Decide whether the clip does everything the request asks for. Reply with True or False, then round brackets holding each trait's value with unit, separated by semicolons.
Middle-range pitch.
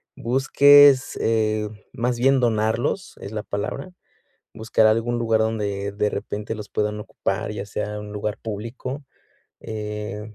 False (110 Hz)